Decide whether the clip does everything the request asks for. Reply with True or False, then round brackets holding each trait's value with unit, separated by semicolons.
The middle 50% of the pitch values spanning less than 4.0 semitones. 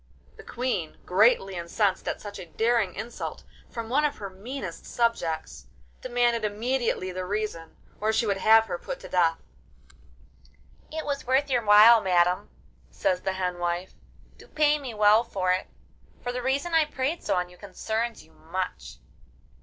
False (4.8 semitones)